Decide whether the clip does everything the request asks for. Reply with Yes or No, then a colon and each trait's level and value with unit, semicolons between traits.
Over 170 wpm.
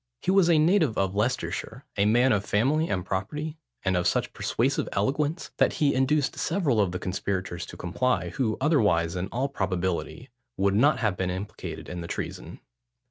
Yes: average, 180 wpm